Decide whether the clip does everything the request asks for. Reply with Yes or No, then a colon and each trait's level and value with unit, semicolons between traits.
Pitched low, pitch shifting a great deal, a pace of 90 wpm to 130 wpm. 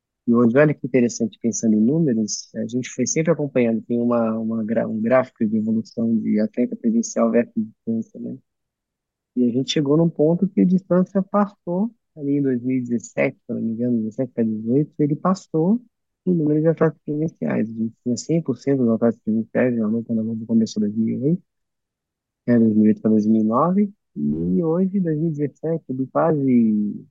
No: low, 130 Hz; wide, 6.8 semitones; average, 175 wpm